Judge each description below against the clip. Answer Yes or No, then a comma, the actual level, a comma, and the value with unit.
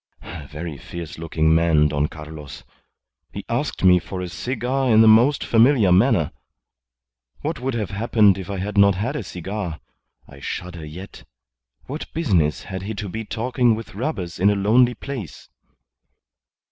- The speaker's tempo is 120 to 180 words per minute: Yes, average, 160 wpm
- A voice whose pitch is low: Yes, low, 100 Hz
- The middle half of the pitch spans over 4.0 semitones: Yes, wide, 5.4 semitones